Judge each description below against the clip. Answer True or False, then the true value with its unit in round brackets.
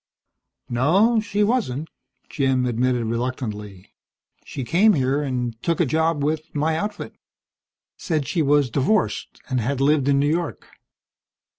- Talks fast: False (135 wpm)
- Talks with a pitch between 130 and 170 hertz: True (140 Hz)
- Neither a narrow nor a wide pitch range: True (4.5 semitones)